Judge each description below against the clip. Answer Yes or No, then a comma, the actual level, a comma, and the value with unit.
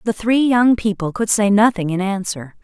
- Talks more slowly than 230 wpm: Yes, fast, 205 wpm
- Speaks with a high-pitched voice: Yes, high, 210 Hz